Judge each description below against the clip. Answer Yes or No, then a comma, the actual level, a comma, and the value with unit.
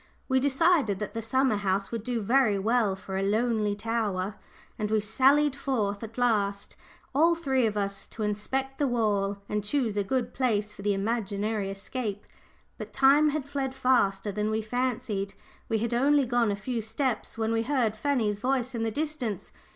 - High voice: Yes, high, 225 Hz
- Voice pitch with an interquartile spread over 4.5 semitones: No, average, 4.2 semitones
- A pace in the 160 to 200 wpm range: Yes, average, 180 wpm